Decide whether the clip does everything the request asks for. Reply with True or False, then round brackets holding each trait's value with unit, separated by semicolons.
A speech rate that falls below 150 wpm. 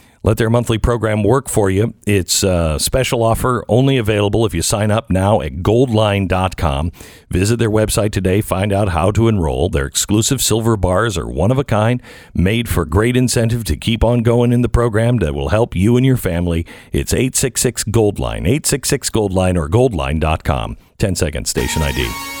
False (180 wpm)